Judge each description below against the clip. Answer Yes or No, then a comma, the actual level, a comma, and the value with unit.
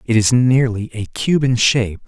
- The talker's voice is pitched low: Yes, low, 120 Hz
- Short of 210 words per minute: Yes, average, 200 wpm